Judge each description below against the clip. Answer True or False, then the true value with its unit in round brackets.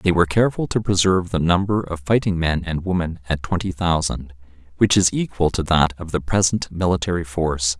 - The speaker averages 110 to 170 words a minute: False (195 wpm)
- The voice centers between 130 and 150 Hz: False (85 Hz)